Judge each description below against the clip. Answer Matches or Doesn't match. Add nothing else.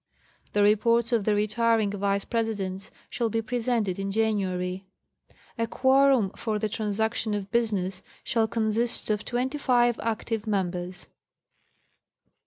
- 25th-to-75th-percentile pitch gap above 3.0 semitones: Doesn't match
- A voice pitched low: Doesn't match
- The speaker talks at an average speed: Doesn't match